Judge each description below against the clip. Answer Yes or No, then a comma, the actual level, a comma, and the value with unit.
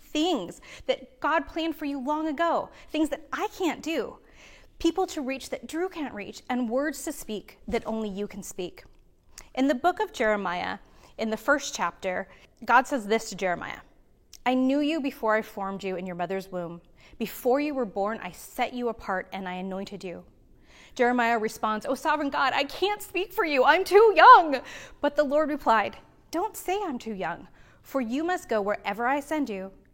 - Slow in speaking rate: No, average, 190 wpm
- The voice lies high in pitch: Yes, very high, 260 Hz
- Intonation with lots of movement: Yes, wide, 6.5 semitones